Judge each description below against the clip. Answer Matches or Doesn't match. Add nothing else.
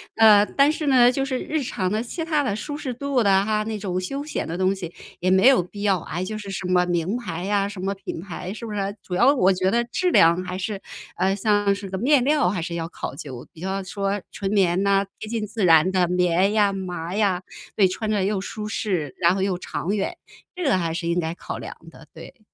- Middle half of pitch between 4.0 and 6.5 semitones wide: Doesn't match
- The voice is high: Matches